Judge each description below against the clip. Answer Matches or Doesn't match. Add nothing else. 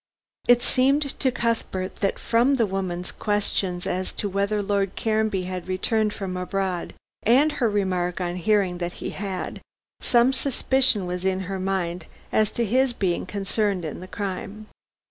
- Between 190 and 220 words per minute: Doesn't match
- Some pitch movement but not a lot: Matches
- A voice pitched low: Doesn't match